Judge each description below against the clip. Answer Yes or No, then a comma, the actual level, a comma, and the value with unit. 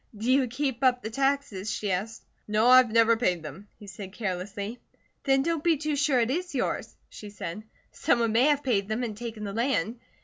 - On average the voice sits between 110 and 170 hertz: No, high, 230 Hz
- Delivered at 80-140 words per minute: No, fast, 205 wpm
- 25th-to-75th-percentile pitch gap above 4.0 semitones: Yes, average, 4.5 semitones